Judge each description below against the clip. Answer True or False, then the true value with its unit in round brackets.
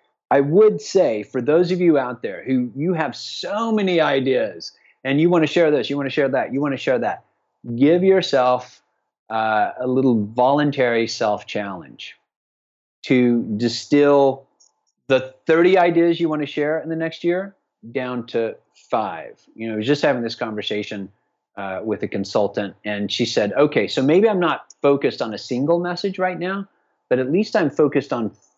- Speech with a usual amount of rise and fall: False (6.3 semitones)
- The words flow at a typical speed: True (185 wpm)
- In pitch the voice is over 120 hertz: True (140 Hz)